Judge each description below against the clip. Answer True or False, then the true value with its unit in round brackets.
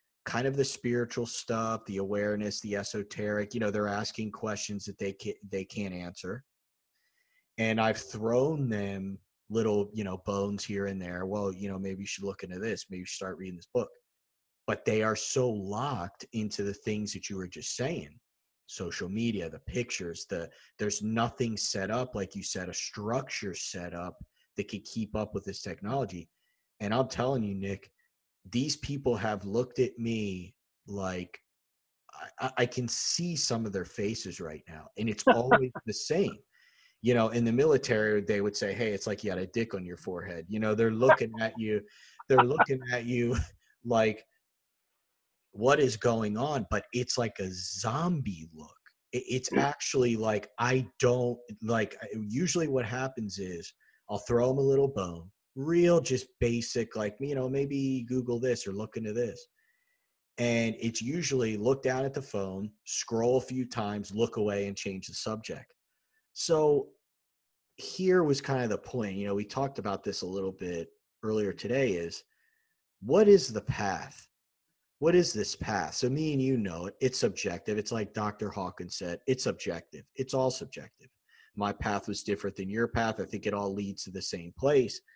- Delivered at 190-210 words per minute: False (180 wpm)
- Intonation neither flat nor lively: True (4.1 semitones)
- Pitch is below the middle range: True (110 Hz)